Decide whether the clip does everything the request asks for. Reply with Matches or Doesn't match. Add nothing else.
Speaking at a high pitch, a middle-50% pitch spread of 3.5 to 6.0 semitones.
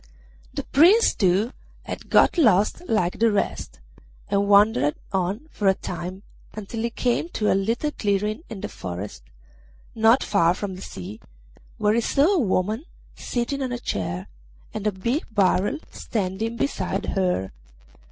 Matches